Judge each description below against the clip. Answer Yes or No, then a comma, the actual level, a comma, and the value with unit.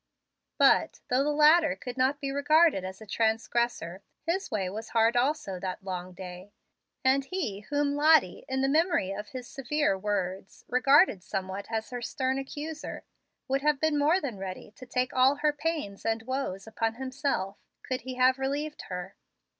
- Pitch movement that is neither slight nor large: No, wide, 6.3 semitones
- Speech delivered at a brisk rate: No, average, 170 wpm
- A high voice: Yes, very high, 255 Hz